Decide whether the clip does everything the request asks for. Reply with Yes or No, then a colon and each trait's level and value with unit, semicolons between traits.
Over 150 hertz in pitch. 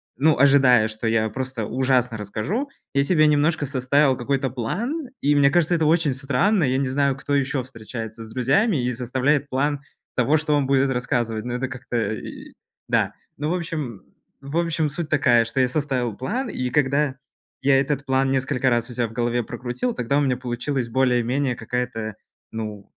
No: low, 130 Hz